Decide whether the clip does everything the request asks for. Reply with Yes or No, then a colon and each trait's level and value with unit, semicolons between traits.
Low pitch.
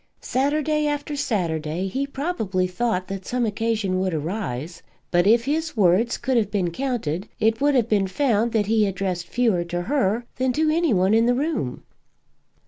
No: high, 220 Hz